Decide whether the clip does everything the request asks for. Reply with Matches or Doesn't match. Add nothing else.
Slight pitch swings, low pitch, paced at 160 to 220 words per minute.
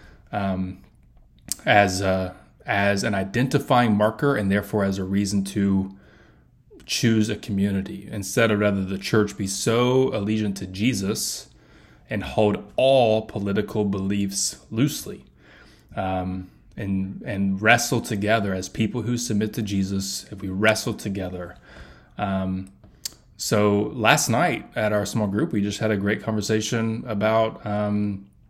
Doesn't match